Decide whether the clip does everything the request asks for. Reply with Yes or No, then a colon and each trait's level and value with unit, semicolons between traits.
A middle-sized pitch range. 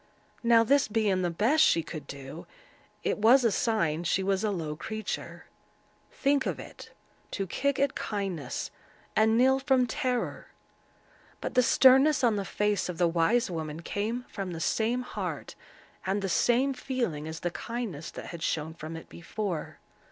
No: wide, 6.5 semitones